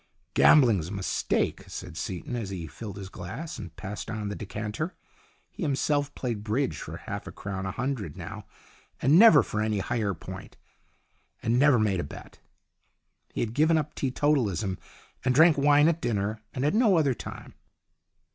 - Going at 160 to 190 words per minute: Yes, average, 175 wpm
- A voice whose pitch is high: No, low, 115 Hz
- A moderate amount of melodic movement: No, wide, 6.4 semitones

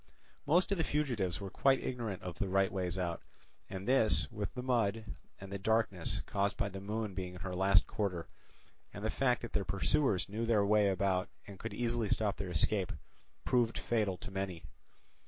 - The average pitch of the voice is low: Yes, low, 100 Hz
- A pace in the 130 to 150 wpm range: No, average, 190 wpm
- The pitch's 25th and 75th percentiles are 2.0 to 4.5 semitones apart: Yes, average, 3.3 semitones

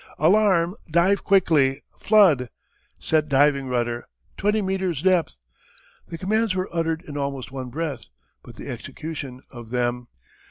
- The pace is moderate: No, slow, 130 wpm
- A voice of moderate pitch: Yes, medium, 160 Hz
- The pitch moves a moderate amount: No, wide, 5.8 semitones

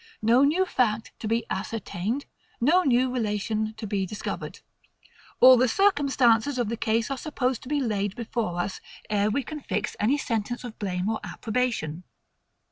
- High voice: Yes, high, 230 Hz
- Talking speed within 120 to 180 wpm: Yes, average, 165 wpm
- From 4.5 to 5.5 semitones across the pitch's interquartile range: No, average, 3.5 semitones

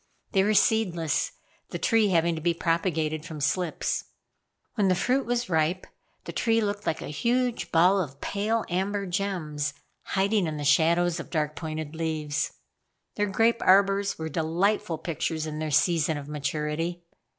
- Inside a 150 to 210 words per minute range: Yes, average, 160 wpm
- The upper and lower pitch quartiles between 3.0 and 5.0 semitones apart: Yes, average, 4.3 semitones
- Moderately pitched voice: Yes, medium, 170 Hz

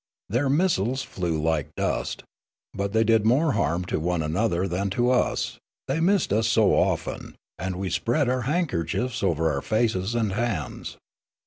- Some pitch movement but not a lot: No, wide, 5.7 semitones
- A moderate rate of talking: Yes, average, 155 wpm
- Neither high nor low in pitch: No, low, 110 Hz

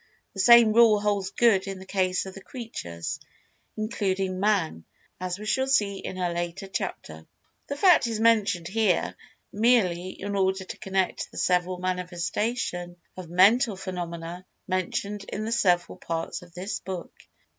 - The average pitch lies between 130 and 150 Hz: No, high, 190 Hz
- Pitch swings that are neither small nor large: Yes, average, 3.2 semitones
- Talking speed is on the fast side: No, average, 155 wpm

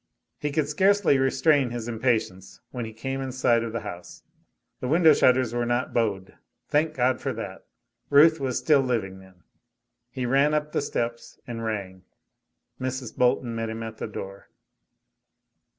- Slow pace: No, average, 165 wpm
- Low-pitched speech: Yes, low, 125 Hz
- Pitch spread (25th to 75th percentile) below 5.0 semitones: Yes, average, 3.6 semitones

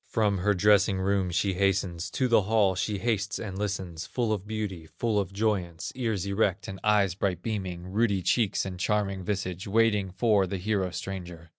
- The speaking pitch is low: Yes, low, 100 Hz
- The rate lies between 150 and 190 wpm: Yes, average, 180 wpm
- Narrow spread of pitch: Yes, narrow, 2.3 semitones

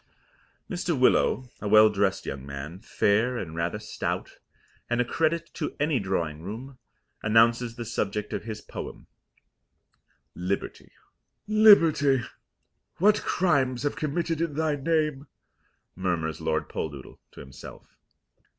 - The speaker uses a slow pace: Yes, slow, 125 wpm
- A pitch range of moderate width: No, wide, 7.7 semitones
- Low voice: Yes, low, 120 Hz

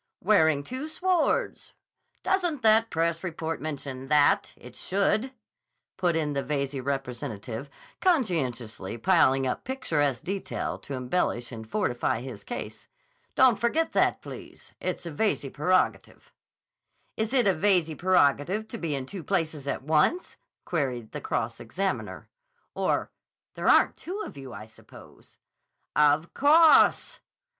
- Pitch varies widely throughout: Yes, wide, 7.9 semitones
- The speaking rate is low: Yes, slow, 130 wpm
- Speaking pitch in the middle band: Yes, medium, 160 Hz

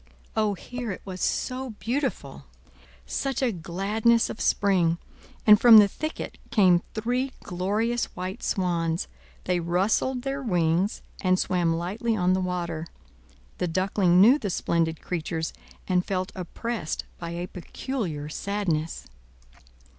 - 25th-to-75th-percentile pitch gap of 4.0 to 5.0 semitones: Yes, average, 4.5 semitones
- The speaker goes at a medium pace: No, slow, 130 wpm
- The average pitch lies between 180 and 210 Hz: Yes, high, 190 Hz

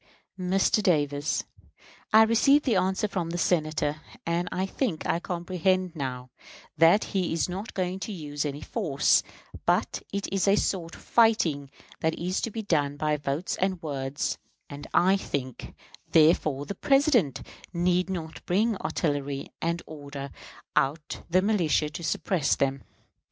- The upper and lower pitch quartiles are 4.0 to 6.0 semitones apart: Yes, average, 4.7 semitones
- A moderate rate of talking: Yes, average, 150 wpm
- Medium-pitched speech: Yes, medium, 170 Hz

